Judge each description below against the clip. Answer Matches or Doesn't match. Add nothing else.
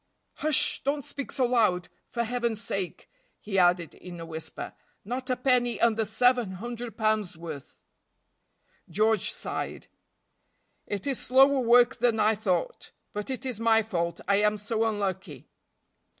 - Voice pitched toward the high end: Matches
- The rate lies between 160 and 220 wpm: Doesn't match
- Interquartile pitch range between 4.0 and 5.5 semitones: Matches